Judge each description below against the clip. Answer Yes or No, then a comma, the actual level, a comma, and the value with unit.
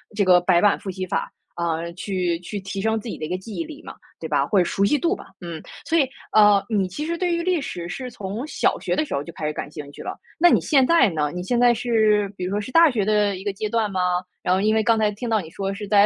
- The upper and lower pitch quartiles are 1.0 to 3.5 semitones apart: No, average, 4.7 semitones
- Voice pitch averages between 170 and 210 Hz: Yes, high, 205 Hz